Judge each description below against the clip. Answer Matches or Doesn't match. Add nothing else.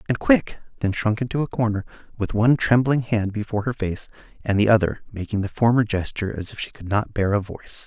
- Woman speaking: Doesn't match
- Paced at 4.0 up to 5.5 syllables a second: Doesn't match